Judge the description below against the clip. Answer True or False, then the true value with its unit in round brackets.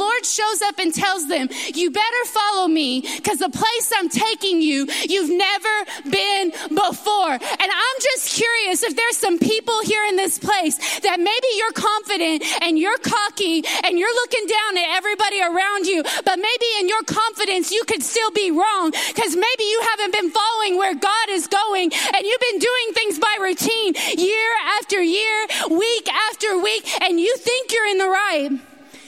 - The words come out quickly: False (180 wpm)